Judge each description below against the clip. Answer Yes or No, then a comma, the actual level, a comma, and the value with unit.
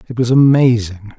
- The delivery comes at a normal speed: Yes, average, 150 wpm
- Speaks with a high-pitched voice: No, low, 120 Hz